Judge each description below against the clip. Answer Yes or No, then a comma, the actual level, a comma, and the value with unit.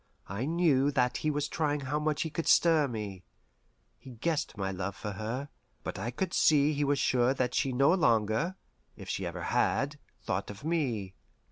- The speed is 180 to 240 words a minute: Yes, average, 190 wpm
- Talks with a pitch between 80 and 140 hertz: Yes, low, 135 Hz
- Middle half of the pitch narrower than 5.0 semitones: No, average, 5.3 semitones